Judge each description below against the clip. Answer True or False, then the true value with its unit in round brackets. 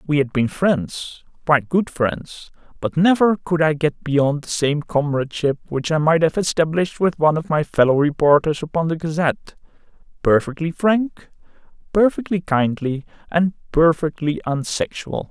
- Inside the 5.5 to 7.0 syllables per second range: False (4.8 syllables/s)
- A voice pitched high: False (160 Hz)